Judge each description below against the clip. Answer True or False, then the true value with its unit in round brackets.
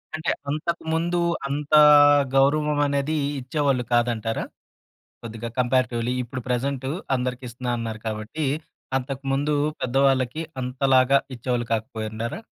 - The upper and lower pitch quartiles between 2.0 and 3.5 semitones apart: True (2.8 semitones)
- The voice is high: False (130 Hz)